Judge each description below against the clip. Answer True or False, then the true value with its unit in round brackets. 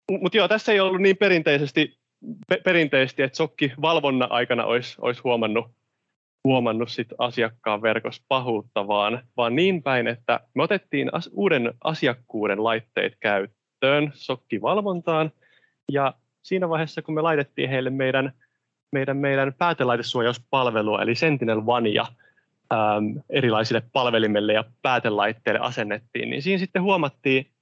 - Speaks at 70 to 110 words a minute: False (120 wpm)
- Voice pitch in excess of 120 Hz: True (135 Hz)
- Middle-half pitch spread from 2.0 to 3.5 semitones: False (4.9 semitones)